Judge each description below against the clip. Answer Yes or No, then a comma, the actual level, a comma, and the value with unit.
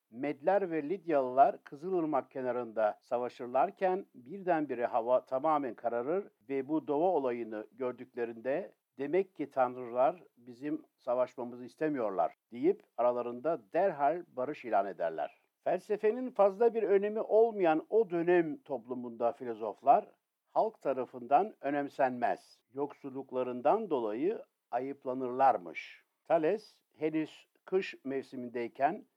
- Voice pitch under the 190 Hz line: Yes, medium, 140 Hz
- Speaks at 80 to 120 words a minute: Yes, slow, 95 wpm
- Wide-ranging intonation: Yes, wide, 6.3 semitones